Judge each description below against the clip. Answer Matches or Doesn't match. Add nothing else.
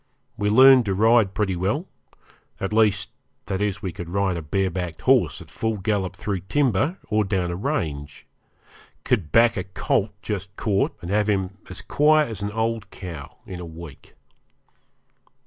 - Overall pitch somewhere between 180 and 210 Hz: Doesn't match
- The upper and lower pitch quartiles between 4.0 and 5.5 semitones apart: Doesn't match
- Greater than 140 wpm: Matches